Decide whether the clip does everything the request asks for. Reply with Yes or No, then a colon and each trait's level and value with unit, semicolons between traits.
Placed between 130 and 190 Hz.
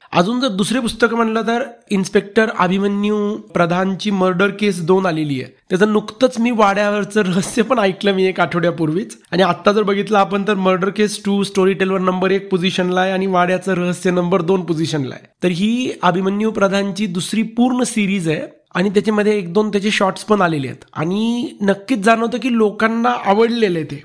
No: high, 200 Hz